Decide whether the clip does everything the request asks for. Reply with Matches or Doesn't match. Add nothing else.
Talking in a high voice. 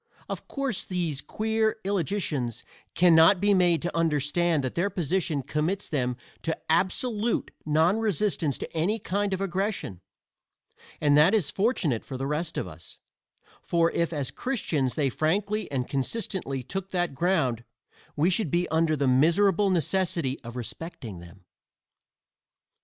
Doesn't match